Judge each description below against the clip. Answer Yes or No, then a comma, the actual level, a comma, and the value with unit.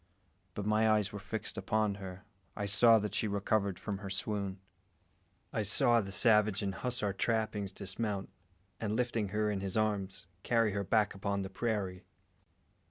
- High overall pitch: No, low, 105 Hz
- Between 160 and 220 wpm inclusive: Yes, average, 165 wpm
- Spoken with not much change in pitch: Yes, narrow, 1.8 semitones